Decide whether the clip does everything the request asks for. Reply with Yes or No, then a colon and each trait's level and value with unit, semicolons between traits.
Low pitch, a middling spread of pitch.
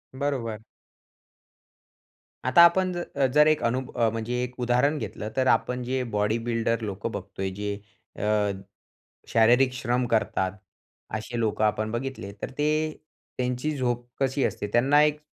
Yes: low, 120 Hz; average, 3.2 semitones